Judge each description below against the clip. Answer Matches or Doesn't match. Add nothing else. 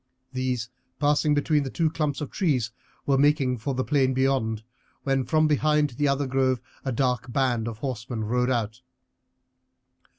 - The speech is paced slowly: Doesn't match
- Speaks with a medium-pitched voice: Doesn't match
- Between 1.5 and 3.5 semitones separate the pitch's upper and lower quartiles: Matches